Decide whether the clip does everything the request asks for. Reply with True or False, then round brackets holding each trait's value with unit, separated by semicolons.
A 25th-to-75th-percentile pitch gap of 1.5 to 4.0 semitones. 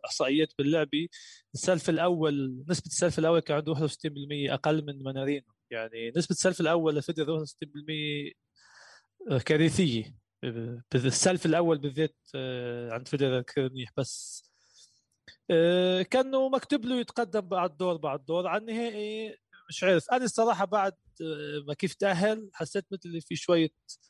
False (4.8 semitones)